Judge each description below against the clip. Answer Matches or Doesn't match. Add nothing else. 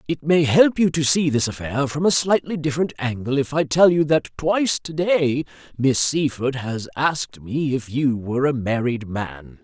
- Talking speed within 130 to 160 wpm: Doesn't match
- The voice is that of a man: Matches